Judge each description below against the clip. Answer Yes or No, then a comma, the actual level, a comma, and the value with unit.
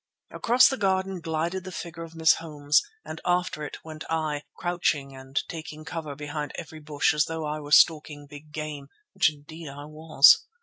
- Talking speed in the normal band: Yes, average, 180 wpm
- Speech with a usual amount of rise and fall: No, narrow, 2.0 semitones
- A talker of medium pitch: Yes, medium, 155 Hz